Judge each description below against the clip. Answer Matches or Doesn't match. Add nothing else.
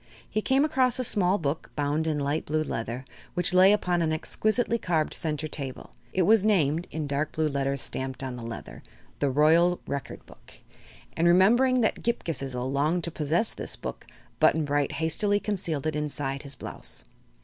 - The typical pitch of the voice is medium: Matches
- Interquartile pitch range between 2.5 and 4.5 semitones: Doesn't match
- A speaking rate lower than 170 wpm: Doesn't match